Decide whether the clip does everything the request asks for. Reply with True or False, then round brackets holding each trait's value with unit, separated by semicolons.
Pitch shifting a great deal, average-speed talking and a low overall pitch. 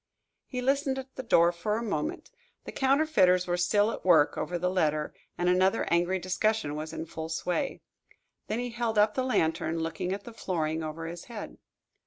False (5.7 semitones; 190 wpm; 185 Hz)